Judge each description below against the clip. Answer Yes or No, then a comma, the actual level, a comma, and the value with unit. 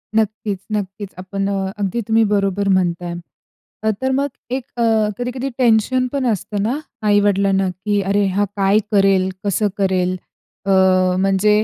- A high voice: Yes, high, 200 Hz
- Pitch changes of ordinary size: No, narrow, 2.2 semitones